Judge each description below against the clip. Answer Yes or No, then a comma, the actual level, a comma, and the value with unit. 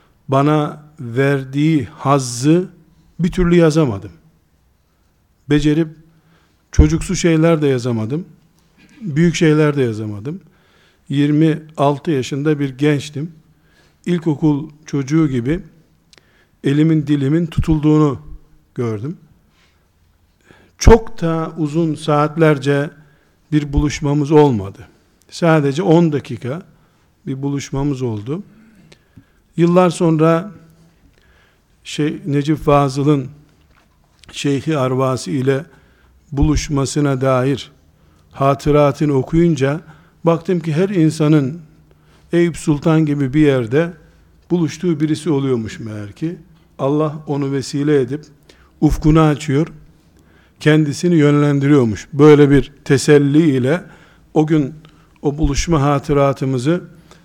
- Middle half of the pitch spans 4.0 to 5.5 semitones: No, average, 3.1 semitones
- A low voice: No, medium, 150 Hz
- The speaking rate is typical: No, slow, 85 wpm